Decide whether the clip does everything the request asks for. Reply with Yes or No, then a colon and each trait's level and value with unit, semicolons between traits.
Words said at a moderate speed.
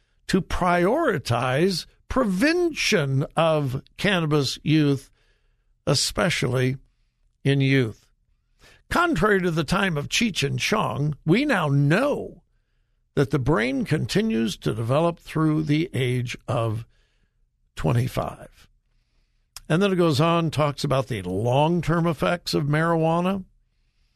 No: slow, 110 wpm